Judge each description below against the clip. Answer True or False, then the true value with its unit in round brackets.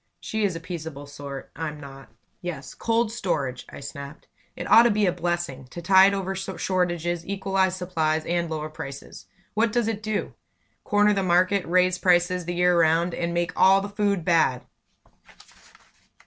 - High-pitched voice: False (175 Hz)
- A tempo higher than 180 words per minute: False (165 wpm)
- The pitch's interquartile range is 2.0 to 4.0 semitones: True (3.4 semitones)